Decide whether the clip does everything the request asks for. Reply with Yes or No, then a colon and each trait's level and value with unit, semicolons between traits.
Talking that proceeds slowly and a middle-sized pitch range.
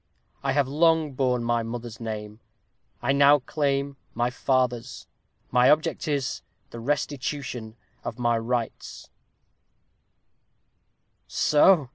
Yes: slow, 100 wpm; average, 3.1 semitones